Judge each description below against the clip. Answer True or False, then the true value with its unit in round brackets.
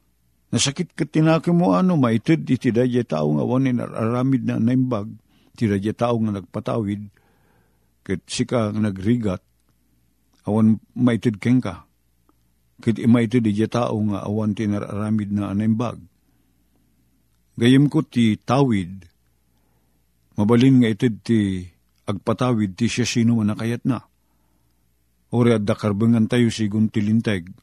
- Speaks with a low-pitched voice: True (110 Hz)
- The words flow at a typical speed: True (125 wpm)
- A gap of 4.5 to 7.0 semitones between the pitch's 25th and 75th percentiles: True (4.9 semitones)